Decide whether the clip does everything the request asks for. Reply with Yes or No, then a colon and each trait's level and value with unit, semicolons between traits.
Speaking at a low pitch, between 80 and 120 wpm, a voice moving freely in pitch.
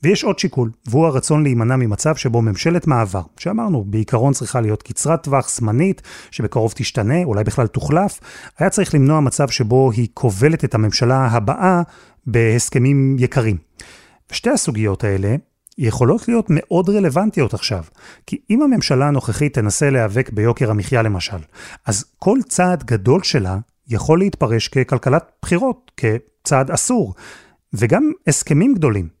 No: low, 130 Hz; average, 135 wpm; wide, 6.5 semitones